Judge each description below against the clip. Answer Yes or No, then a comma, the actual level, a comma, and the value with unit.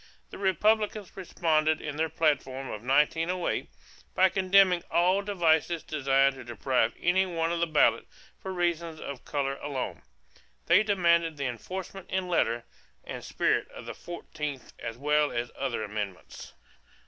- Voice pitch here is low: No, medium, 160 Hz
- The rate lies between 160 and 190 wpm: No, average, 150 wpm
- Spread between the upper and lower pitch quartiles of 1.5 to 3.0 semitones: No, average, 4.8 semitones